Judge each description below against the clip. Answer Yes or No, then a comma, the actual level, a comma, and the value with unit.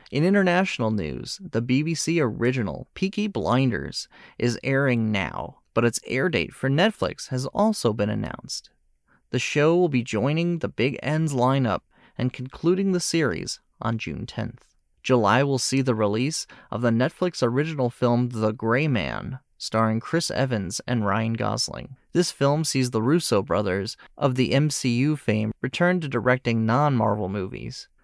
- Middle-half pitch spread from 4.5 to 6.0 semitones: Yes, average, 4.8 semitones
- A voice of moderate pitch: No, low, 125 Hz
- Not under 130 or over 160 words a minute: Yes, average, 150 wpm